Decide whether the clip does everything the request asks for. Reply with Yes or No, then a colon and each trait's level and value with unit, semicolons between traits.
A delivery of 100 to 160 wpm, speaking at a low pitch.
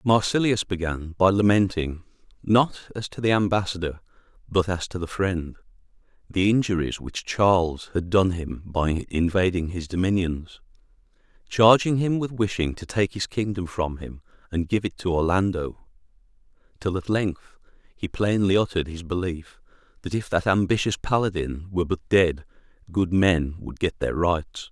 Yes: average, 150 wpm; very low, 95 Hz